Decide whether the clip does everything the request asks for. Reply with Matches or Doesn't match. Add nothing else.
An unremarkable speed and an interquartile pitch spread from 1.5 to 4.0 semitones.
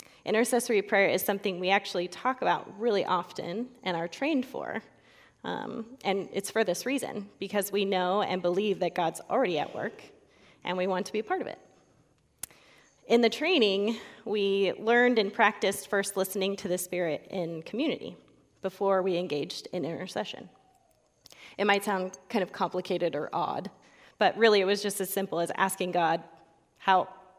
Matches